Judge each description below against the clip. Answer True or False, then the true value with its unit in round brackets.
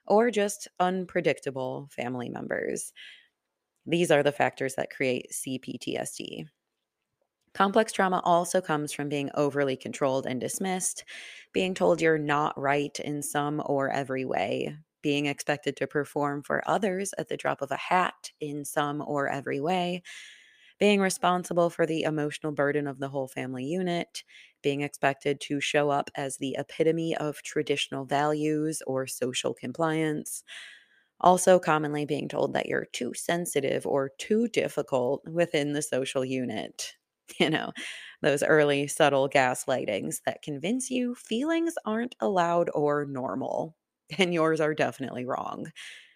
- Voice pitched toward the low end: False (150 Hz)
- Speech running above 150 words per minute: False (140 wpm)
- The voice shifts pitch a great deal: False (3.9 semitones)